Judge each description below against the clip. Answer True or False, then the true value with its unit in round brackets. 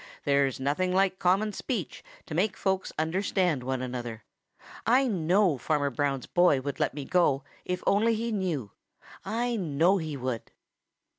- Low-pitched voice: False (170 Hz)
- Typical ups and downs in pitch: False (5.8 semitones)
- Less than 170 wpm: True (150 wpm)